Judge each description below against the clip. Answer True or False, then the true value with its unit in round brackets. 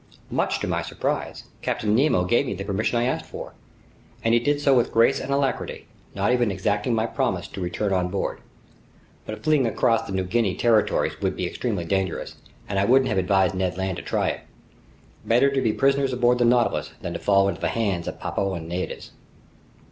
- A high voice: False (110 Hz)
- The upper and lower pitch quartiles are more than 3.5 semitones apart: True (4.5 semitones)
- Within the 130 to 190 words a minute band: False (200 wpm)